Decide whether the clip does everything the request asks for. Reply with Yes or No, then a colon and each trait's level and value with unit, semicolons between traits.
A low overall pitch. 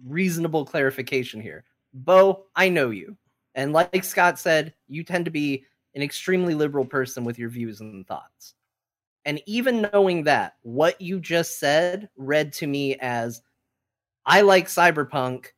No: medium, 145 Hz